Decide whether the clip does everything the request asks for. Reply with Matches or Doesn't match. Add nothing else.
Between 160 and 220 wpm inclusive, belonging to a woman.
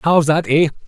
Doesn't match